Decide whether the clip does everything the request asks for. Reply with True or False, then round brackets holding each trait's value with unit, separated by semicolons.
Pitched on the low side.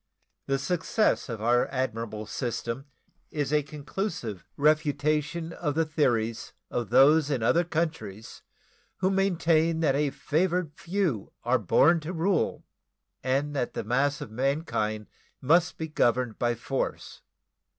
False (145 Hz)